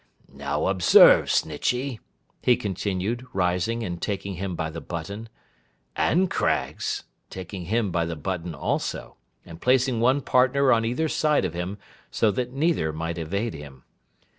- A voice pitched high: No, low, 100 Hz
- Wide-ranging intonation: Yes, wide, 6.5 semitones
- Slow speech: No, average, 145 wpm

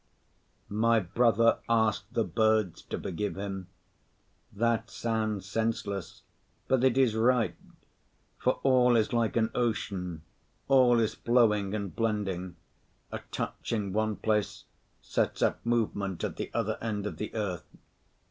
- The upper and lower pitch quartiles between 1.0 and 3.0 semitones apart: Yes, narrow, 2.5 semitones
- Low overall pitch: Yes, low, 110 Hz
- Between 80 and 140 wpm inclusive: Yes, slow, 135 wpm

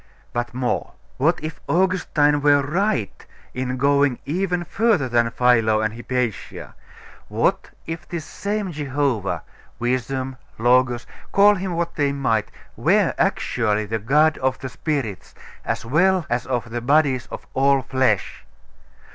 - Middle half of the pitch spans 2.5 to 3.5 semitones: No, average, 4.6 semitones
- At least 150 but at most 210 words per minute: No, slow, 135 wpm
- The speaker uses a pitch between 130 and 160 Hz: Yes, low, 135 Hz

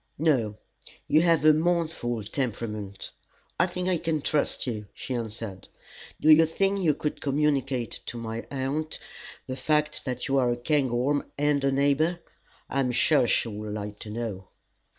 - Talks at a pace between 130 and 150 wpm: No, average, 165 wpm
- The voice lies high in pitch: No, low, 135 Hz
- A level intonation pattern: No, average, 4.8 semitones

